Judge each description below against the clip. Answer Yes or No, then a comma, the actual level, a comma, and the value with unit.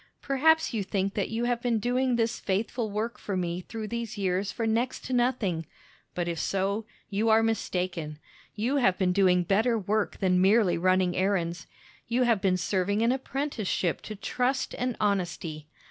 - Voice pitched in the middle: No, high, 205 Hz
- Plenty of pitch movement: No, average, 4.2 semitones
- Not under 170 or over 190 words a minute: Yes, average, 175 wpm